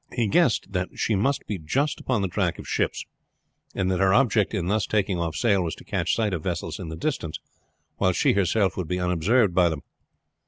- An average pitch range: Yes, average, 3.6 semitones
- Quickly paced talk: Yes, fast, 220 wpm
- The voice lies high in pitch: No, very low, 95 Hz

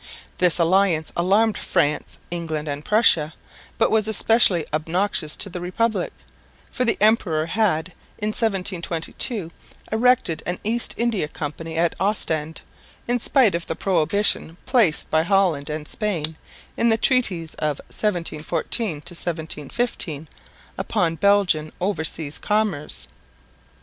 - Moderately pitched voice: Yes, medium, 180 Hz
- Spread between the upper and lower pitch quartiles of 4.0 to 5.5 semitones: Yes, average, 5.1 semitones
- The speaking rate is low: Yes, slow, 120 wpm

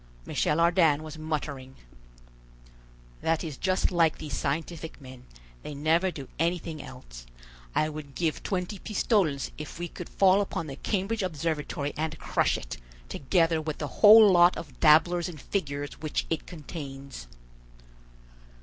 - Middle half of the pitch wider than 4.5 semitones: No, average, 3.3 semitones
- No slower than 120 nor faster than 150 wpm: Yes, average, 140 wpm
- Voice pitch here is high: No, medium, 160 Hz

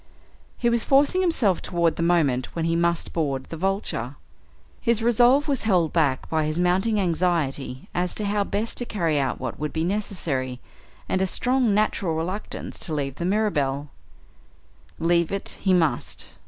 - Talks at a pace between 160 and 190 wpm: Yes, average, 170 wpm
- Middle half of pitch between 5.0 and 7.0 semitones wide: Yes, wide, 5.4 semitones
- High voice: No, medium, 175 Hz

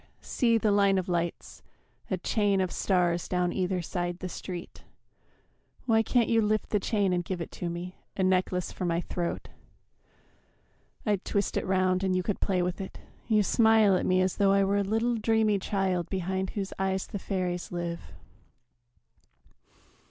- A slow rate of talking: No, average, 175 wpm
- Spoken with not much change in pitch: Yes, narrow, 2.2 semitones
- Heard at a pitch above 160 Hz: Yes, high, 190 Hz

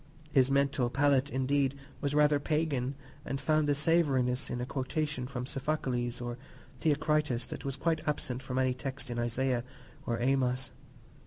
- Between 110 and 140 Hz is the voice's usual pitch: Yes, low, 135 Hz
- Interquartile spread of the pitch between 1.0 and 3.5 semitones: Yes, narrow, 2.5 semitones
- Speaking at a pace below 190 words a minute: Yes, average, 155 wpm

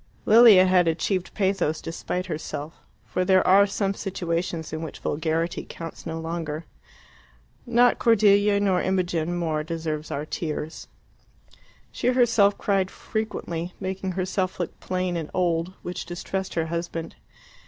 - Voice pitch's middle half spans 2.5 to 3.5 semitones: Yes, average, 2.9 semitones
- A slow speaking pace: Yes, slow, 130 wpm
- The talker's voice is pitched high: No, medium, 180 Hz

